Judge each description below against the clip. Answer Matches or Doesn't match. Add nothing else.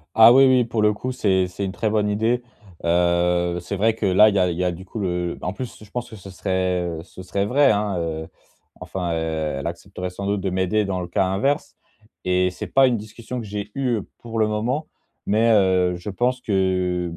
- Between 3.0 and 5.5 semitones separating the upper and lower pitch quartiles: Matches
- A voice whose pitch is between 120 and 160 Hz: Doesn't match